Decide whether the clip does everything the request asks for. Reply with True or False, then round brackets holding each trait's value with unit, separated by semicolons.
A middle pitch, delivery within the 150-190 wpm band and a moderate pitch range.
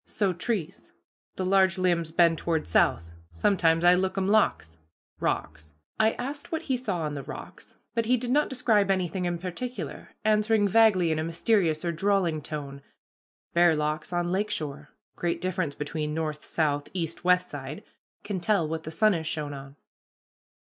True (175 Hz; 170 wpm; 4.6 semitones)